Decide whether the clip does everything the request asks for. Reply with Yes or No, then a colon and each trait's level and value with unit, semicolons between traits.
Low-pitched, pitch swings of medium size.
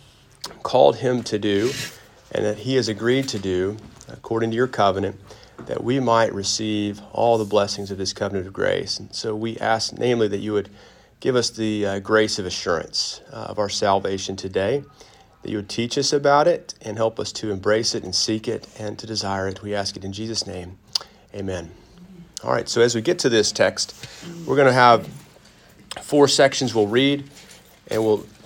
Yes: low, 110 Hz; average, 3.1 semitones